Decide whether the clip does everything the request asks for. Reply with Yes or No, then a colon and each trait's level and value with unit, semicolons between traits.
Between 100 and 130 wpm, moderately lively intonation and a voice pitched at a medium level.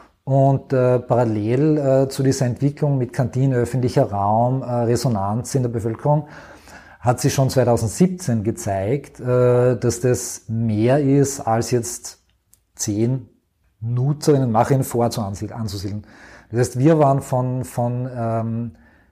No: slow, 125 wpm; average, 3.0 semitones; low, 125 Hz